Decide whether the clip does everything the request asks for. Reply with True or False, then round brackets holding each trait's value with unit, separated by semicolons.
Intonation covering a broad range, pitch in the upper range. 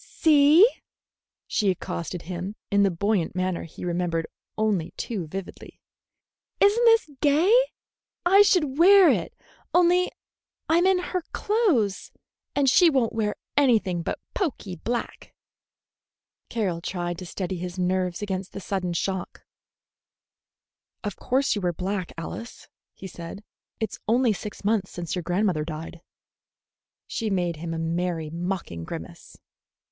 True (7.5 semitones; 195 Hz)